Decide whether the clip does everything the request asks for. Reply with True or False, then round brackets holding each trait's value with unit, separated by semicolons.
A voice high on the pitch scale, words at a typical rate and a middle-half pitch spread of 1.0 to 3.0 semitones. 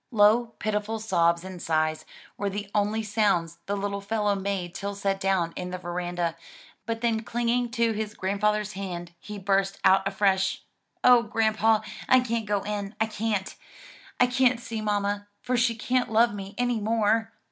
True (205 Hz; 170 wpm; 2.6 semitones)